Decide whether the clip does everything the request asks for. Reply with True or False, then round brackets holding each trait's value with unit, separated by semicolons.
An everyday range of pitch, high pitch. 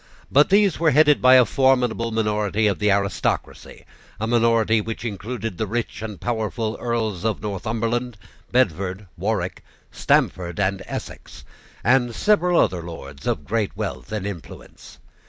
False (3.3 semitones; 110 Hz)